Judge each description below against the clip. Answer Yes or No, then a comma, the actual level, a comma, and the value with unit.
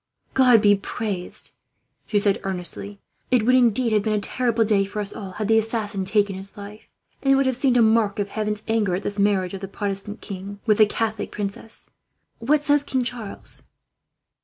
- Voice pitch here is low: No, high, 210 Hz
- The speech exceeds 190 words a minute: Yes, average, 200 wpm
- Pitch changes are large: No, narrow, 2.4 semitones